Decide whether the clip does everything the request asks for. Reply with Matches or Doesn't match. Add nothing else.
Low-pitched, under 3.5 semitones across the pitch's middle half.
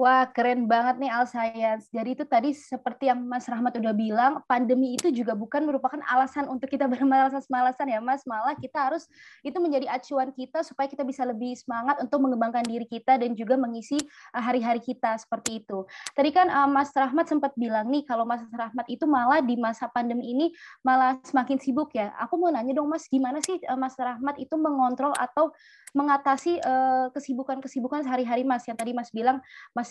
Doesn't match